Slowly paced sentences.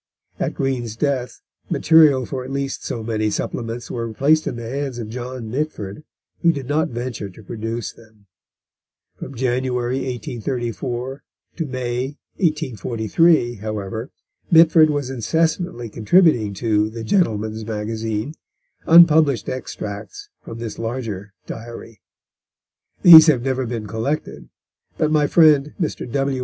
Yes: slow, 125 wpm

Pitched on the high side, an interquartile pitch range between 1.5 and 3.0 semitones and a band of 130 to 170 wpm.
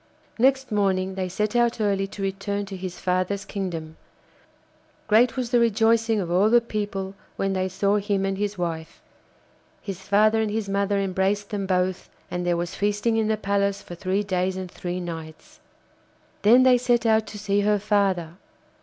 No: high, 200 Hz; narrow, 2.4 semitones; average, 180 wpm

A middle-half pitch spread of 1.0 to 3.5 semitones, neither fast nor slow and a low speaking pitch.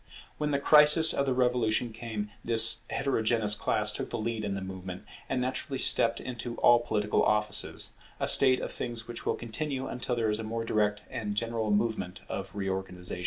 Yes: average, 2.7 semitones; average, 185 wpm; low, 115 Hz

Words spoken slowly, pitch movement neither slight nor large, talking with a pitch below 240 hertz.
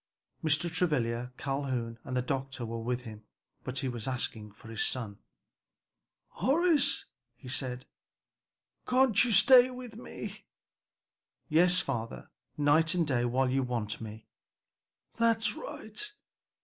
No: slow, 125 wpm; wide, 7.1 semitones; low, 135 Hz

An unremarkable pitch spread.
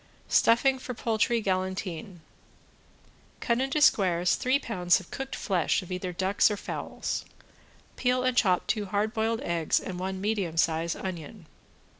Yes: average, 4.3 semitones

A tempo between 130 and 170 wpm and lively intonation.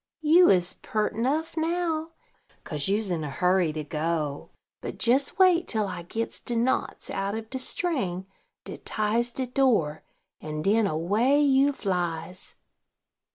Yes: average, 150 wpm; wide, 7.5 semitones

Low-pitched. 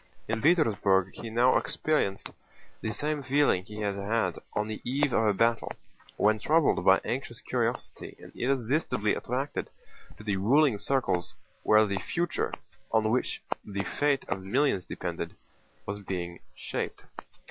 Yes: low, 110 Hz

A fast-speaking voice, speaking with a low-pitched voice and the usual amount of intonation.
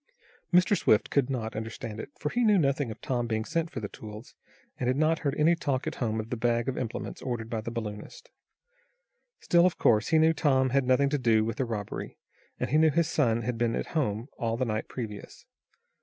Yes: fast, 225 wpm; low, 125 Hz; average, 4.8 semitones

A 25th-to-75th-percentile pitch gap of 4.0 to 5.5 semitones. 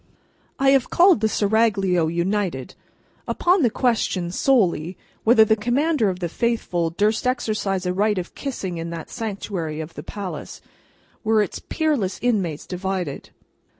Yes: average, 4.8 semitones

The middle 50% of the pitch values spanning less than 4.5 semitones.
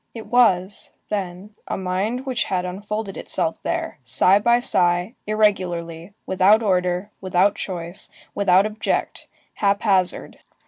Yes: average, 2.8 semitones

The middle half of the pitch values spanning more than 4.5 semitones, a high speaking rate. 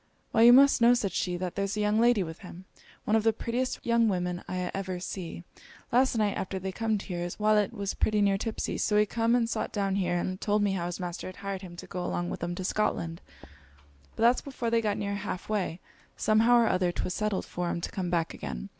No: average, 3.6 semitones; fast, 245 wpm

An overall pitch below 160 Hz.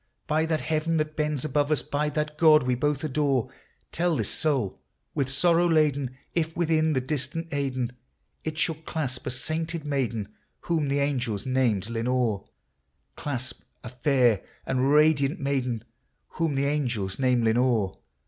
Yes: medium, 140 Hz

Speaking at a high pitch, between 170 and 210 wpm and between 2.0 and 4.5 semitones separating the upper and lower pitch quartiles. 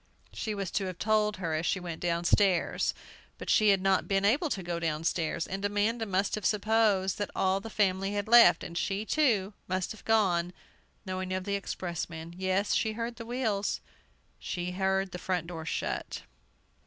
Yes: high, 195 Hz; average, 180 wpm; average, 2.9 semitones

